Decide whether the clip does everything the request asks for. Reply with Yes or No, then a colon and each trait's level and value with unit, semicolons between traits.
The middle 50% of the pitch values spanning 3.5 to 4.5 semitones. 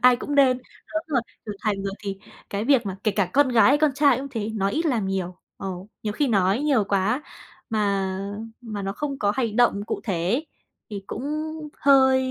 No: average, 5.2 semitones